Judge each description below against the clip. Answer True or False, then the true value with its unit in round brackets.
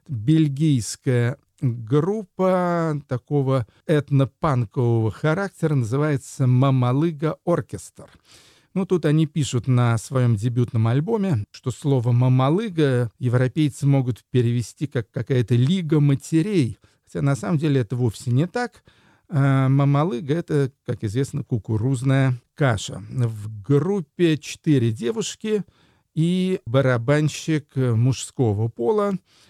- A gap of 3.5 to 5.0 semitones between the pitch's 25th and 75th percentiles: True (4.1 semitones)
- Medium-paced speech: False (100 wpm)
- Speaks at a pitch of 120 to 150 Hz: True (135 Hz)